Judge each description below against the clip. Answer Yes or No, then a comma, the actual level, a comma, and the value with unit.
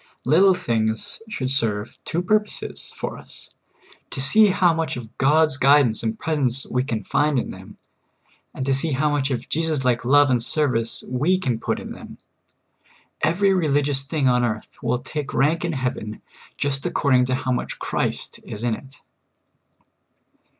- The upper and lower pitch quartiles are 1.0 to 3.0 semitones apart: No, average, 4.0 semitones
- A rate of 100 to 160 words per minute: No, average, 170 wpm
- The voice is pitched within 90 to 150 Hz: Yes, low, 135 Hz